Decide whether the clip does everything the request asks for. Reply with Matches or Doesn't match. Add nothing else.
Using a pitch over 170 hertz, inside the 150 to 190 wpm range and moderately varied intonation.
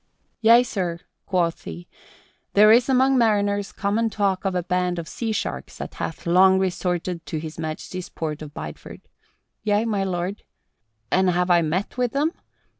Matches